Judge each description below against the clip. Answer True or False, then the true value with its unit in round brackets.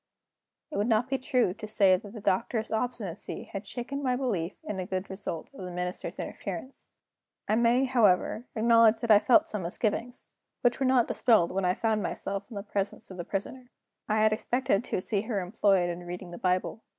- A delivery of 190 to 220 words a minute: True (200 wpm)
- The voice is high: True (215 Hz)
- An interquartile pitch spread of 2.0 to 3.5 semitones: False (4.3 semitones)